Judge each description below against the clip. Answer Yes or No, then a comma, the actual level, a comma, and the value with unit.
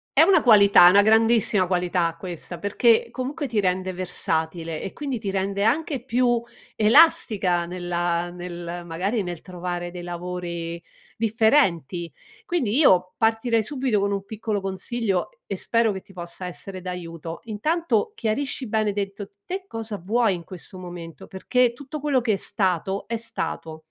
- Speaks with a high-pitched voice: Yes, high, 195 Hz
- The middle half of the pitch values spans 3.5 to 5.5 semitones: Yes, average, 4.6 semitones